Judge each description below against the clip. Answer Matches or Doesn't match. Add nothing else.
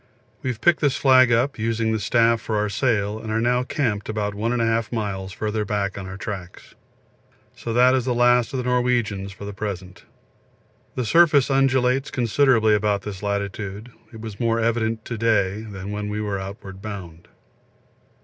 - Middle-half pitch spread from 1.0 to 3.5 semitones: Matches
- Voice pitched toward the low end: Matches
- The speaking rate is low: Doesn't match